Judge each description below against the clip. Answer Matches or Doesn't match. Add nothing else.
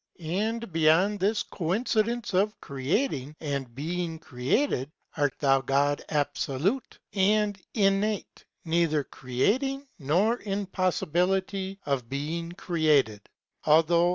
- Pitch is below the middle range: Doesn't match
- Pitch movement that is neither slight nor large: Doesn't match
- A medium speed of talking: Doesn't match